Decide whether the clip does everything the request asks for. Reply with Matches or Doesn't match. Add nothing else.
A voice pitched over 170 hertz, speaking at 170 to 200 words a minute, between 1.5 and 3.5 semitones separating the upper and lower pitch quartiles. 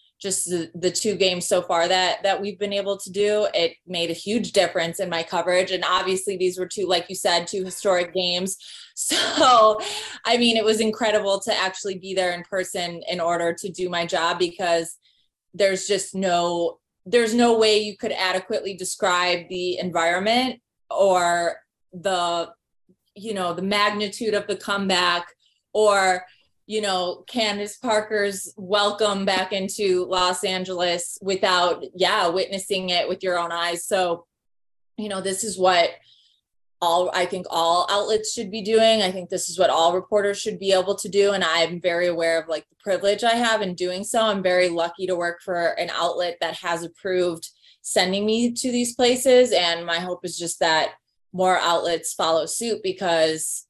Matches